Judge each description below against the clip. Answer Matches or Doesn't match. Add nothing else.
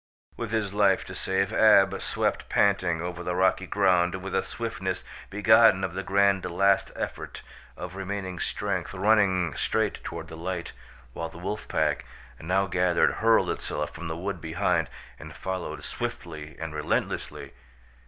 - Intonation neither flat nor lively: Doesn't match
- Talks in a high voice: Doesn't match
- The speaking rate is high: Doesn't match